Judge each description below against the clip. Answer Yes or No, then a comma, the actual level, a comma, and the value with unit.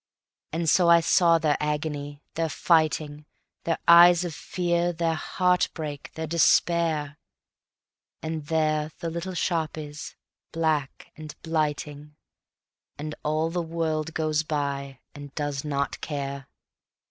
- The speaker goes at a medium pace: No, slow, 125 wpm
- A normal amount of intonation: No, narrow, 2.0 semitones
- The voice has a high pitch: No, medium, 155 Hz